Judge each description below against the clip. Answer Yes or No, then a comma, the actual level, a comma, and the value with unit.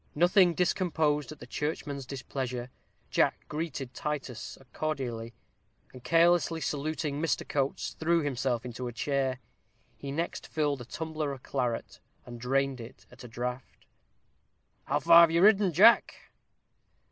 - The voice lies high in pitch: No, medium, 140 Hz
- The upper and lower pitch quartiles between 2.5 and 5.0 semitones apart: Yes, average, 4.1 semitones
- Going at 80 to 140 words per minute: Yes, slow, 135 wpm